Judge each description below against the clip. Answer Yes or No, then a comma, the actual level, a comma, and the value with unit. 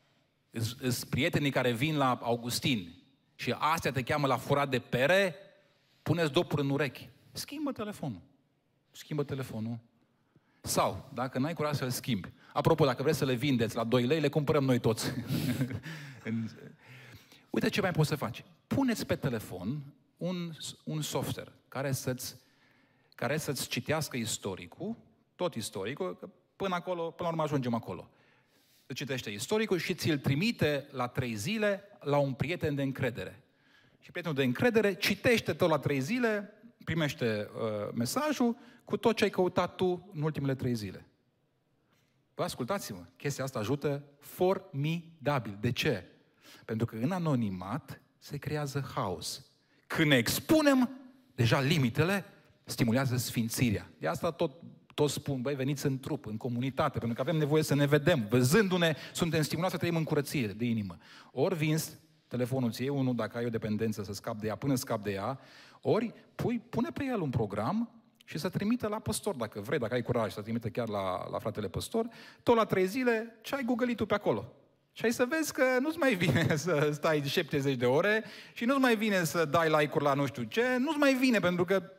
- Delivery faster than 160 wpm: Yes, fast, 170 wpm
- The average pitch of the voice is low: No, medium, 145 Hz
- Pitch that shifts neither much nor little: No, wide, 6.0 semitones